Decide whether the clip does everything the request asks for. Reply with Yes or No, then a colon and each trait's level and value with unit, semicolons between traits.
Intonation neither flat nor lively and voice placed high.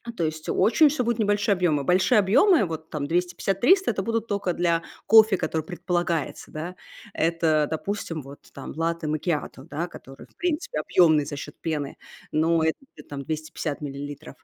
No: average, 4.5 semitones; medium, 170 Hz